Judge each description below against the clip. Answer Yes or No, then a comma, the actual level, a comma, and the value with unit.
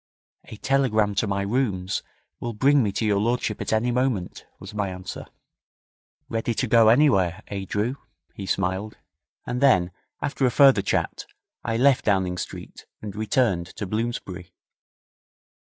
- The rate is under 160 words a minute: Yes, average, 150 wpm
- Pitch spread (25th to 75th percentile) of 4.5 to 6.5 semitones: No, average, 4.1 semitones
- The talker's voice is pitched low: Yes, low, 110 Hz